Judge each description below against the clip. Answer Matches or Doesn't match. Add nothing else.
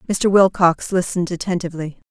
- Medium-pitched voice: Matches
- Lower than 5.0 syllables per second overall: Doesn't match